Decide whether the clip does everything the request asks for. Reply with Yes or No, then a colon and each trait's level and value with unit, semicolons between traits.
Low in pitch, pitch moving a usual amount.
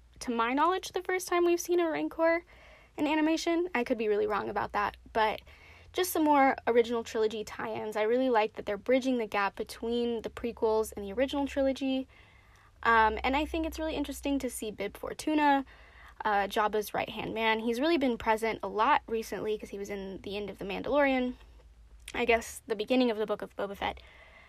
No: high, 235 Hz; average, 4.8 semitones